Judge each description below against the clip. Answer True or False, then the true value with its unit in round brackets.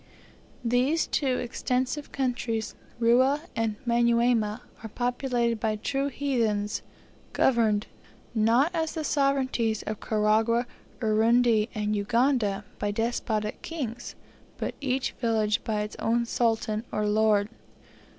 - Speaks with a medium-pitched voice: False (235 Hz)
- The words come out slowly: True (110 wpm)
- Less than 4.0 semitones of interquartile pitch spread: True (2.7 semitones)